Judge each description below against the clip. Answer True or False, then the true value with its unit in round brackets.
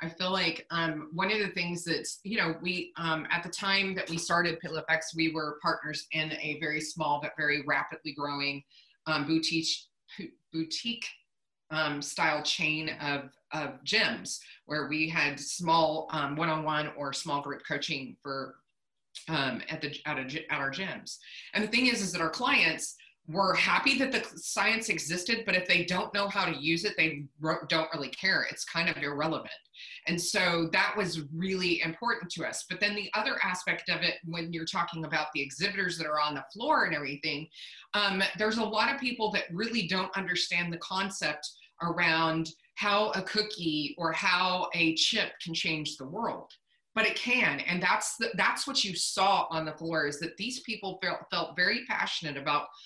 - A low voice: False (165 Hz)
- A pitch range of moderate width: True (3.8 semitones)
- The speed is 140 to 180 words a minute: False (195 wpm)